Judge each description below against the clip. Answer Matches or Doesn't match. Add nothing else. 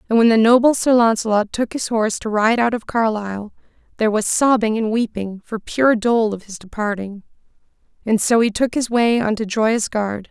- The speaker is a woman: Matches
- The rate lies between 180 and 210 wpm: Matches